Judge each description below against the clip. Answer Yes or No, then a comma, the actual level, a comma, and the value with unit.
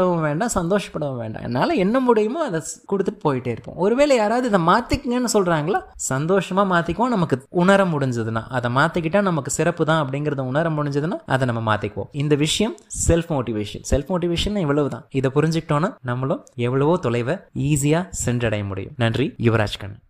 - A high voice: No, medium, 150 Hz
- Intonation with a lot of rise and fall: Yes, wide, 6.7 semitones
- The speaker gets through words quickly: Yes, fast, 150 wpm